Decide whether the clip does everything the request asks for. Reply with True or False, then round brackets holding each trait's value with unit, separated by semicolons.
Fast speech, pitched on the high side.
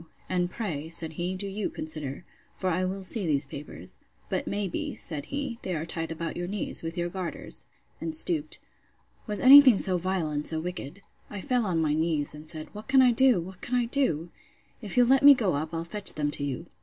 False (225 wpm; 180 Hz)